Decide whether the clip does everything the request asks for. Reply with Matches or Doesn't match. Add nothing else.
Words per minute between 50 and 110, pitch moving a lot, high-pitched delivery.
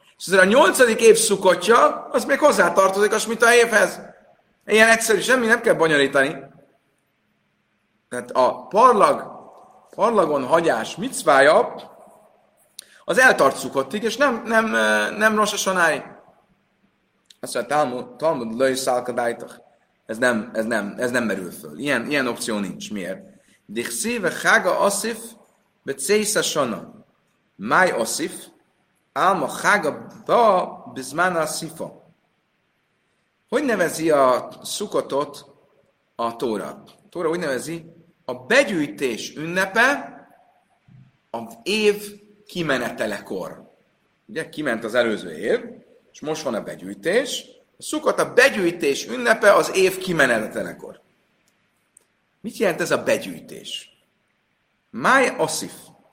Matches